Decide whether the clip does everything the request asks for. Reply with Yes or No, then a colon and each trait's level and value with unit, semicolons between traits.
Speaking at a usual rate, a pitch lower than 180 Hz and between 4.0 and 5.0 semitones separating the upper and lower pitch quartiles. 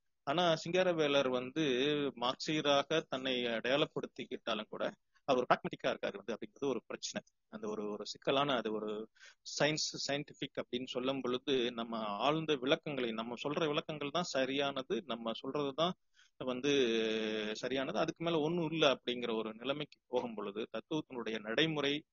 Yes: average, 120 wpm; low, 135 Hz; average, 4.4 semitones